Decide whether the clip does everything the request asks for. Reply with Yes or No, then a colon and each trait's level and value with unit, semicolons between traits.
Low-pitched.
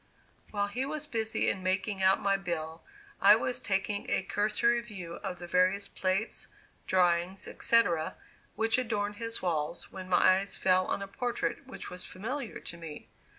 No: high, 195 Hz